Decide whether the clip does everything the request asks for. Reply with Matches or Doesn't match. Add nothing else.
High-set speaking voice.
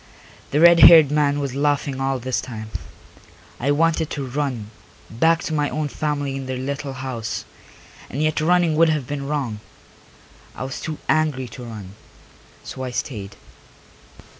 Doesn't match